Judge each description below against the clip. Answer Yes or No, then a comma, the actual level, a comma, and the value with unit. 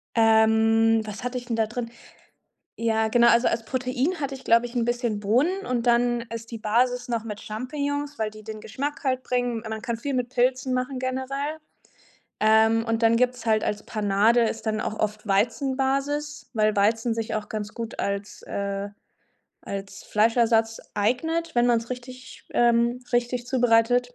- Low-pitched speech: No, high, 235 Hz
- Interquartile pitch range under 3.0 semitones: Yes, narrow, 2.4 semitones